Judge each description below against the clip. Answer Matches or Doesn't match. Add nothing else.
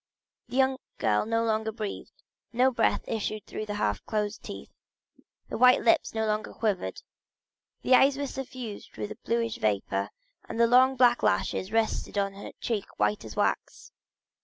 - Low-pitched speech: Doesn't match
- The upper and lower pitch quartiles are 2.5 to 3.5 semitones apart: Matches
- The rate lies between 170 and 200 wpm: Doesn't match